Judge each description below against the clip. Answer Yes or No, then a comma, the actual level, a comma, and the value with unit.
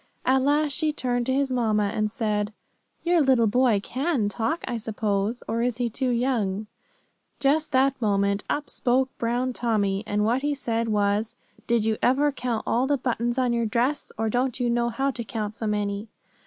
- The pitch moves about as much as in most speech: Yes, average, 3.5 semitones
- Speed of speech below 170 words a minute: No, average, 190 wpm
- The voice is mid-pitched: No, high, 235 Hz